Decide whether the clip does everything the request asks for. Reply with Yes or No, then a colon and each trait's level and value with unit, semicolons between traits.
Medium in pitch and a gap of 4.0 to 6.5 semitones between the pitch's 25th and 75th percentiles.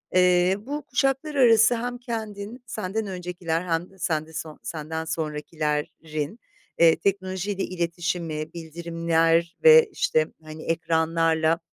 Yes: medium, 170 Hz; average, 4.4 semitones